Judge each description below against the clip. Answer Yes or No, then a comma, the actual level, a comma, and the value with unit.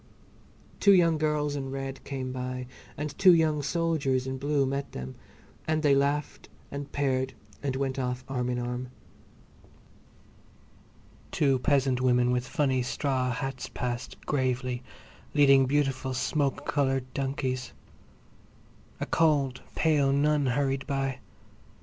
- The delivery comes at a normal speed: No, slow, 125 wpm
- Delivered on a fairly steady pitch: Yes, narrow, 2.0 semitones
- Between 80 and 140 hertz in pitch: Yes, low, 135 Hz